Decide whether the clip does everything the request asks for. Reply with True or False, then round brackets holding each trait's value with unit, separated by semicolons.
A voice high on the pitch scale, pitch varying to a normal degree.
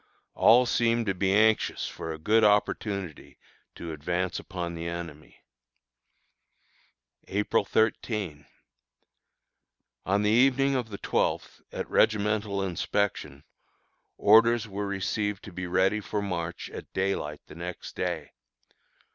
False (100 Hz; 3.8 semitones)